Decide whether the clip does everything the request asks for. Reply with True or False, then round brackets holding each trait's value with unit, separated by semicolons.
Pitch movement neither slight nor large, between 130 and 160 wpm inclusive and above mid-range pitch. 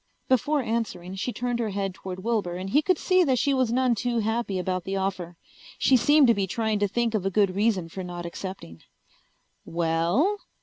False (4.8 semitones; 205 wpm; 210 Hz)